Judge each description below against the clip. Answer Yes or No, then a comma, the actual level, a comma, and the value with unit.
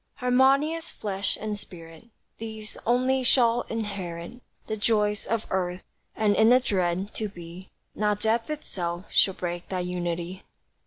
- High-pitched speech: Yes, high, 210 Hz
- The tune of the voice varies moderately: Yes, average, 4.4 semitones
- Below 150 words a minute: Yes, average, 140 wpm